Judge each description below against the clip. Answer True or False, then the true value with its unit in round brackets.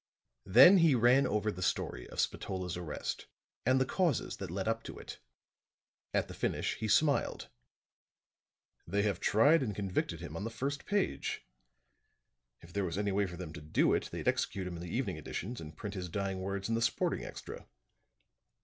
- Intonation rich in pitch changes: False (4.6 semitones)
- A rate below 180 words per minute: False (185 wpm)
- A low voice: True (100 Hz)